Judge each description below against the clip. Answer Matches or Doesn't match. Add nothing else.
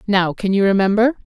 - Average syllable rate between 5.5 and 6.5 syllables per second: Matches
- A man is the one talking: Doesn't match